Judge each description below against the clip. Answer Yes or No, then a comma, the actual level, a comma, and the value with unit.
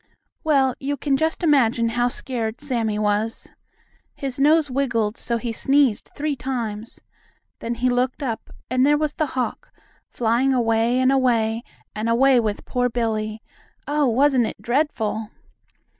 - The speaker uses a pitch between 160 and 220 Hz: No, high, 245 Hz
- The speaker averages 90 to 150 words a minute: Yes, average, 145 wpm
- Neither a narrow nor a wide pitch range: Yes, average, 3.2 semitones